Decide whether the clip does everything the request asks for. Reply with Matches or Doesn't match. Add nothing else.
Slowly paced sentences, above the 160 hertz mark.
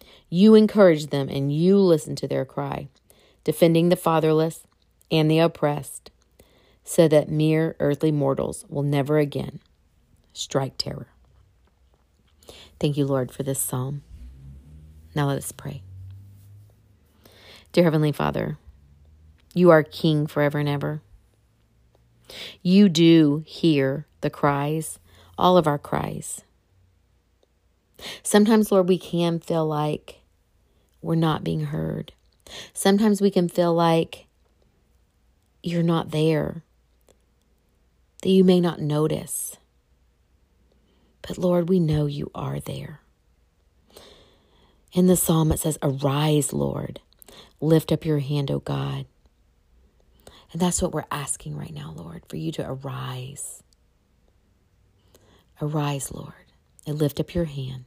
Doesn't match